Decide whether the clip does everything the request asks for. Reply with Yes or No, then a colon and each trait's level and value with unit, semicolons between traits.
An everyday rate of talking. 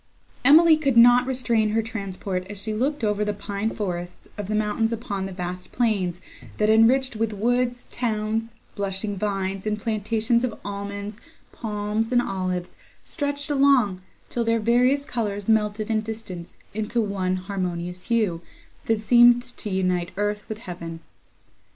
Yes: average, 150 wpm